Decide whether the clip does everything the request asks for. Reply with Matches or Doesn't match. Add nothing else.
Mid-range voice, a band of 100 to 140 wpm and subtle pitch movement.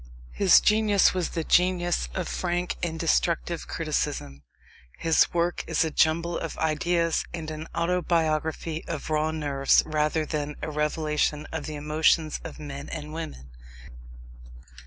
Matches